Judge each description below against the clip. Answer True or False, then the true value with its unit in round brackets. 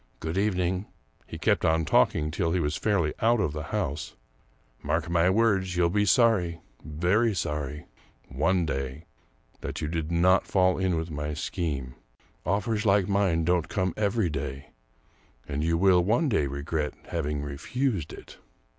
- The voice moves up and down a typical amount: True (4.3 semitones)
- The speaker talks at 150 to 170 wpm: False (180 wpm)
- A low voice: True (85 Hz)